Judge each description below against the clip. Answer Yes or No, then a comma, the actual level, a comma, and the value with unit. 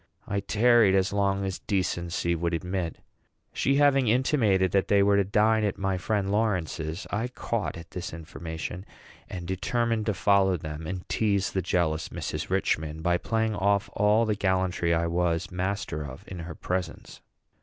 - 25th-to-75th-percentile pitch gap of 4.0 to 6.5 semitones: No, average, 3.3 semitones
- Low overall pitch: Yes, very low, 95 Hz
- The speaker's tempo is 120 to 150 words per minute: No, average, 165 wpm